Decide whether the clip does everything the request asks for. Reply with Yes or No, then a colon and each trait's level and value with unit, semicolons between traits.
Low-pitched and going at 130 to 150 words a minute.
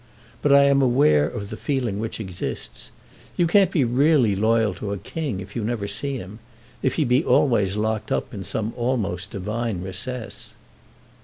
No: low, 115 Hz; average, 175 wpm